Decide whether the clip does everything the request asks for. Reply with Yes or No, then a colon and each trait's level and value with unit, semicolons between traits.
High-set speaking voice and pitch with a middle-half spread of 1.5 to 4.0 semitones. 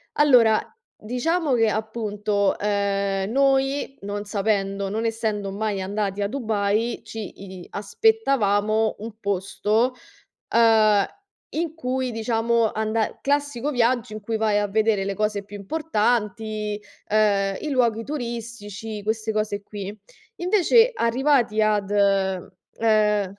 Yes: high, 215 Hz; average, 2.7 semitones